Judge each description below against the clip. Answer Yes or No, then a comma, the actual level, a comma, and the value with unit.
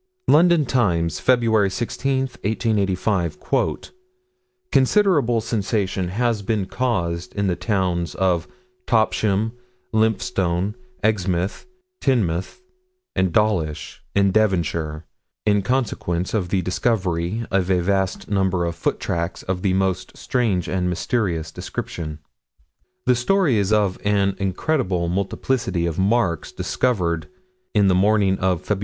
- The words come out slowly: Yes, slow, 115 wpm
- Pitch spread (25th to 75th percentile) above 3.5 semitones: Yes, average, 3.9 semitones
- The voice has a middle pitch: No, very low, 95 Hz